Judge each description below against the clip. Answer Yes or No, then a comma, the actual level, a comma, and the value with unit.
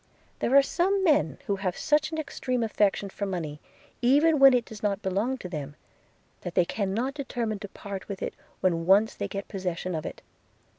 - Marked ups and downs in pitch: Yes, wide, 5.9 semitones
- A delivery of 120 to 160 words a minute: No, average, 195 wpm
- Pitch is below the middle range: No, high, 205 Hz